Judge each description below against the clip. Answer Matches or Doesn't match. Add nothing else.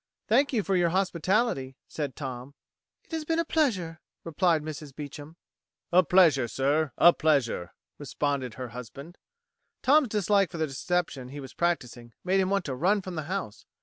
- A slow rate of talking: Doesn't match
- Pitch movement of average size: Doesn't match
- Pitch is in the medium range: Matches